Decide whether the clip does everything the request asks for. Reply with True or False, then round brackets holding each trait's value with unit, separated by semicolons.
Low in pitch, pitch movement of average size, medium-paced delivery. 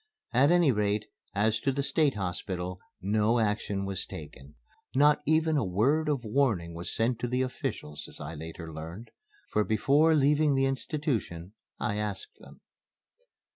False (110 Hz; 6.8 semitones; 155 wpm)